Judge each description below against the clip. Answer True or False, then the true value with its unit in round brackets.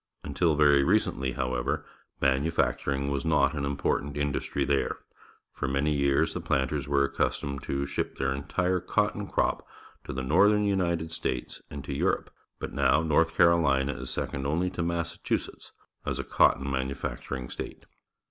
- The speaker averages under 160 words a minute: True (150 wpm)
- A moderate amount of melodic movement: True (3.3 semitones)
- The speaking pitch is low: True (70 Hz)